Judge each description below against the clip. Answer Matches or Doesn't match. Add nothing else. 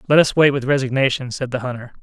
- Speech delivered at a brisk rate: Matches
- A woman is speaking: Doesn't match